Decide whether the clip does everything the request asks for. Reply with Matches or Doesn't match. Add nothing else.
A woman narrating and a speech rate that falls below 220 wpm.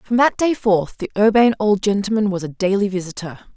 Matches